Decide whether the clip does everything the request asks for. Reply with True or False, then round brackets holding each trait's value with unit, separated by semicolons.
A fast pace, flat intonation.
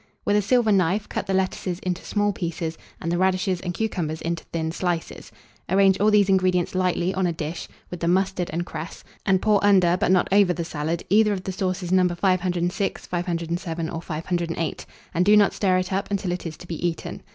True (210 wpm; 2.1 semitones)